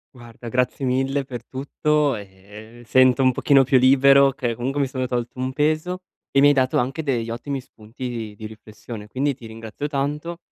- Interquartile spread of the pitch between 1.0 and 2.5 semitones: No, average, 2.9 semitones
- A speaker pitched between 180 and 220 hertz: No, low, 130 Hz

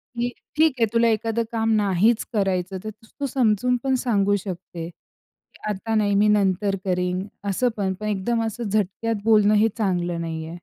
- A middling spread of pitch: Yes, average, 3.2 semitones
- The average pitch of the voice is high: Yes, high, 210 Hz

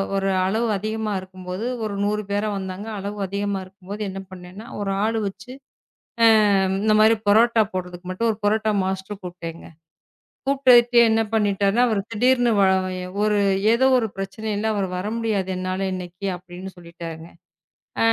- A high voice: Yes, high, 200 Hz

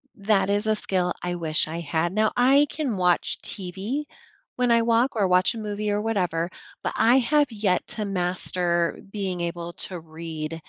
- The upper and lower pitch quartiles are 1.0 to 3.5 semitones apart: No, average, 4.3 semitones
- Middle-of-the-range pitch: No, high, 195 Hz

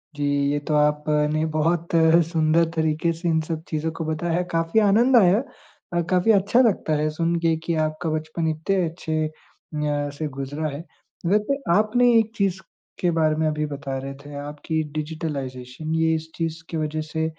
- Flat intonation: Yes, narrow, 2.0 semitones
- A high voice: No, medium, 160 Hz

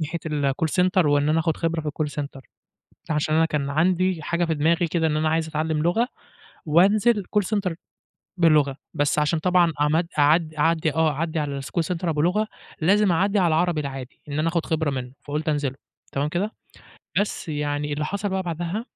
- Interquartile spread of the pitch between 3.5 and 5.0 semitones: No, average, 2.8 semitones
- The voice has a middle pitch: Yes, medium, 160 Hz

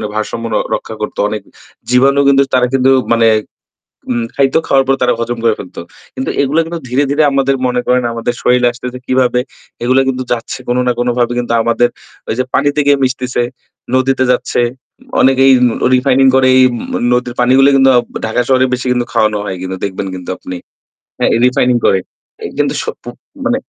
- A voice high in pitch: No, low, 125 Hz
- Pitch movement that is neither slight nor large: No, narrow, 1.9 semitones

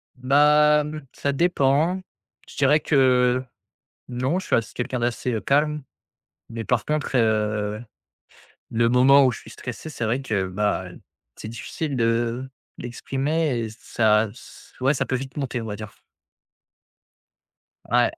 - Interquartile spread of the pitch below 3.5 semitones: No, average, 3.8 semitones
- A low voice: Yes, low, 125 Hz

